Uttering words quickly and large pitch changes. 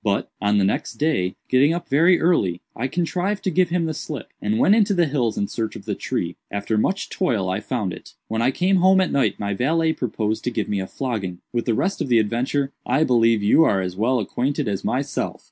Yes: fast, 235 wpm; wide, 7.6 semitones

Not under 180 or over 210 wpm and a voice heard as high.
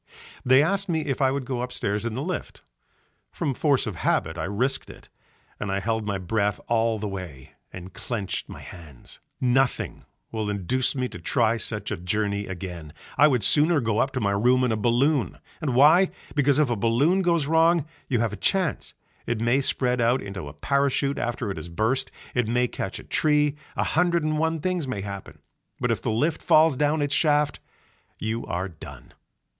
No: average, 200 wpm; low, 125 Hz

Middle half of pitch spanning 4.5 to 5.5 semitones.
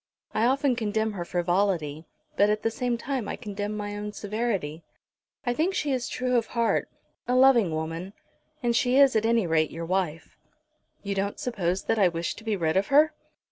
Yes: average, 5.1 semitones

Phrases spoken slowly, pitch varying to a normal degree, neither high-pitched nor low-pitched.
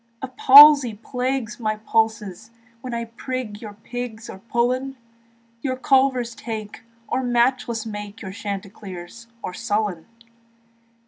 No: slow, 120 wpm; average, 3.3 semitones; high, 230 Hz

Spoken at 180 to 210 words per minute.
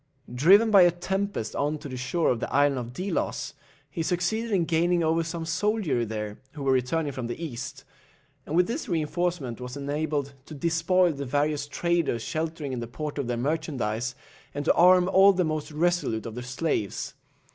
Yes: average, 190 wpm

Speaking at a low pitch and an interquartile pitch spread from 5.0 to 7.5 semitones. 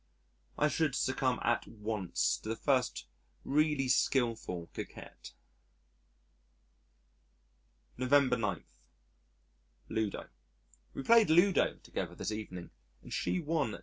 Yes: low, 130 Hz; average, 5.3 semitones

